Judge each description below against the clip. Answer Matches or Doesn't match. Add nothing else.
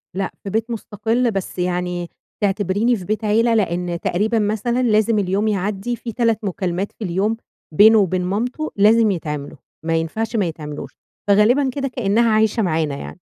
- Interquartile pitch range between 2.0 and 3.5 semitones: Doesn't match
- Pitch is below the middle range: Doesn't match